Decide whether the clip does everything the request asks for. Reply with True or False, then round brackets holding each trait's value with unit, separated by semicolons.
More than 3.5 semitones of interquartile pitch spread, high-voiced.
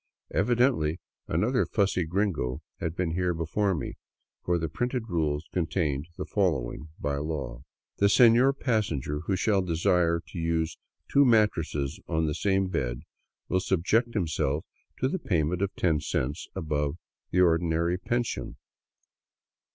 False (4.4 semitones; 85 Hz)